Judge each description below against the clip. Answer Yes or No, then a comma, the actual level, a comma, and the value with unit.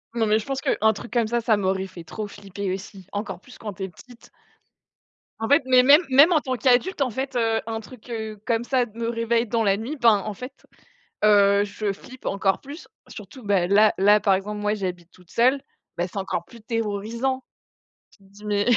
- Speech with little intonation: No, average, 3.5 semitones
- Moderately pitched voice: No, high, 220 Hz